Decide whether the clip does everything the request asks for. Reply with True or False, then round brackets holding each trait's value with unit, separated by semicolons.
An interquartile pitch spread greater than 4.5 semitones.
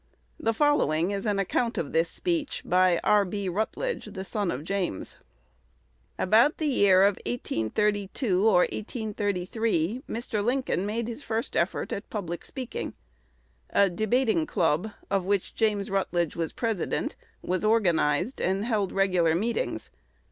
False (3.9 semitones)